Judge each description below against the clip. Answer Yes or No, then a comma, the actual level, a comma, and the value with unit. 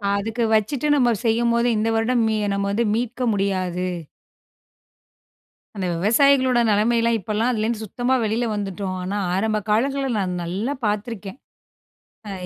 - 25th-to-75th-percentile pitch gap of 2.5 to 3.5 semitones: Yes, average, 3.1 semitones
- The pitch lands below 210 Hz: No, high, 220 Hz